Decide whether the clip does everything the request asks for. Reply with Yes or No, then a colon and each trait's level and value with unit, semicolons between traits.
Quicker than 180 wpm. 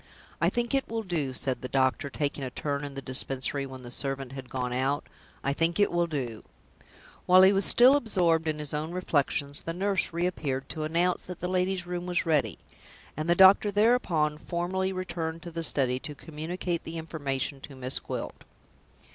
Yes: average, 195 wpm